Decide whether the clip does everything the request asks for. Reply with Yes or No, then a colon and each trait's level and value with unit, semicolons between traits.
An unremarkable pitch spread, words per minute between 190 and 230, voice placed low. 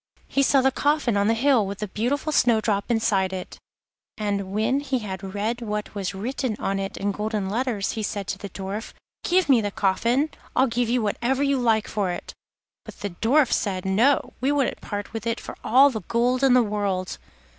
No: average, 4.2 semitones; fast, 205 wpm; high, 220 Hz